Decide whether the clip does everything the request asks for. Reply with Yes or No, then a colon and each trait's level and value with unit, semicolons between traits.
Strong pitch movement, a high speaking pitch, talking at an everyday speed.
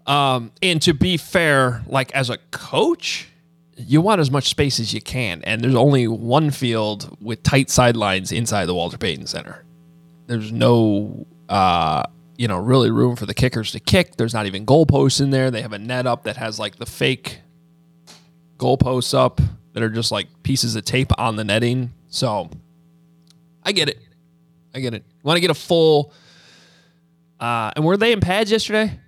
No: wide, 6.0 semitones; low, 135 Hz; average, 190 wpm